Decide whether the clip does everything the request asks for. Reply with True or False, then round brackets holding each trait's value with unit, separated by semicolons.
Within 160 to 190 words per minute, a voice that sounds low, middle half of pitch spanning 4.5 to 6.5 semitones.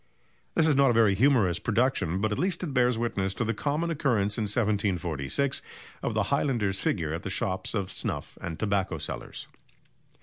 True (180 wpm; 105 Hz; 5.3 semitones)